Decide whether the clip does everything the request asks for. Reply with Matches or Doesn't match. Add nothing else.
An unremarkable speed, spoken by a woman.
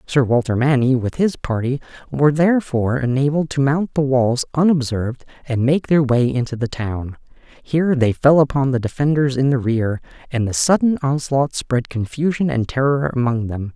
Doesn't match